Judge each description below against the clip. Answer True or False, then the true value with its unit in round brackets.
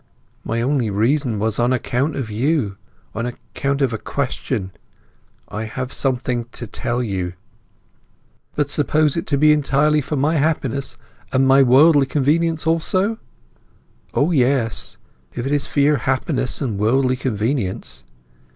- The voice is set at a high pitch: False (135 Hz)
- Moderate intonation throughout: True (3.9 semitones)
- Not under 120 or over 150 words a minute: True (140 wpm)